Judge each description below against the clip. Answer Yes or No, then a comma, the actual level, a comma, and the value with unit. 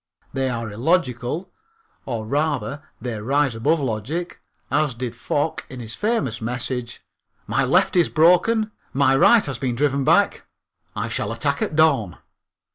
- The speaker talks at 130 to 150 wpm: Yes, average, 145 wpm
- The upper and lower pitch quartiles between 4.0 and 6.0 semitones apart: Yes, average, 5.1 semitones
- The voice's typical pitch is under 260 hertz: Yes, low, 135 Hz